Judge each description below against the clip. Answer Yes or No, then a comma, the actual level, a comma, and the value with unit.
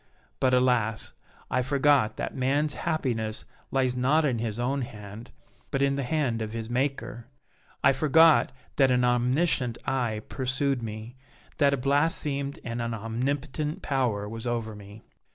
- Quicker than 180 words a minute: No, average, 145 wpm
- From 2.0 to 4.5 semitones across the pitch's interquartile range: Yes, average, 3.4 semitones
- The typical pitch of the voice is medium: No, low, 125 Hz